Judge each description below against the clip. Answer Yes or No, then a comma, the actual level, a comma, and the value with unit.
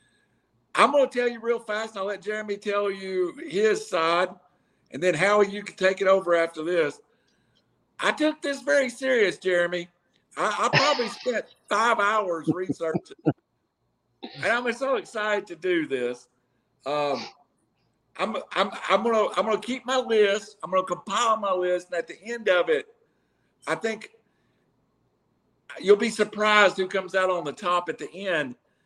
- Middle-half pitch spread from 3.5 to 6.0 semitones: Yes, average, 4.8 semitones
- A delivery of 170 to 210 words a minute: Yes, average, 175 wpm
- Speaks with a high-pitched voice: Yes, high, 205 Hz